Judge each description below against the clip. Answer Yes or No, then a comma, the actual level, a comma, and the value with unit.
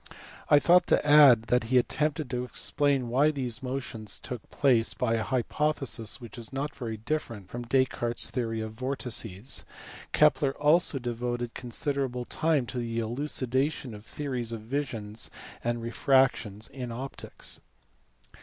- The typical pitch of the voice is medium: No, low, 125 Hz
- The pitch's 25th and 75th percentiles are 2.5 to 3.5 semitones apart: Yes, average, 3.0 semitones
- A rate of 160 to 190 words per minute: No, average, 145 wpm